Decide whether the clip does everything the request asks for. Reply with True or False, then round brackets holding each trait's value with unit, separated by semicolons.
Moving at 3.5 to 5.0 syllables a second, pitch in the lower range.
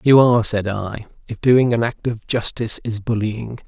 True (4.9 syllables/s; 115 Hz)